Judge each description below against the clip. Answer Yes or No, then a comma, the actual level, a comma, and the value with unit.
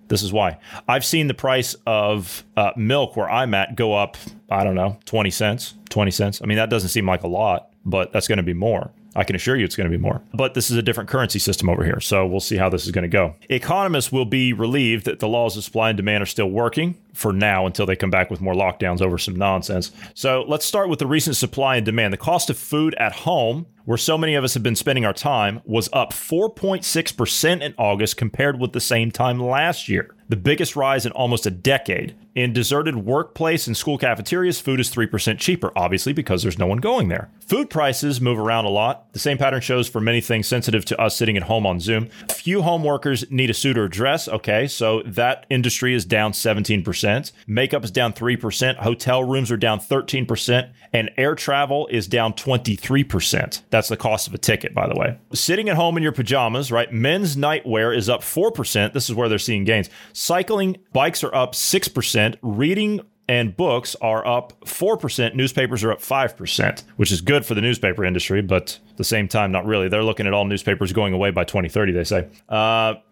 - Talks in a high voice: No, low, 115 Hz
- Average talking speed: No, fast, 220 wpm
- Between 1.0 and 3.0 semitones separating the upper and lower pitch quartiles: No, average, 4.3 semitones